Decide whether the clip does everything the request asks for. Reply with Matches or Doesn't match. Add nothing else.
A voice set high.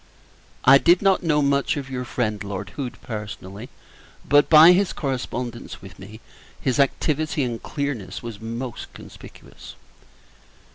Doesn't match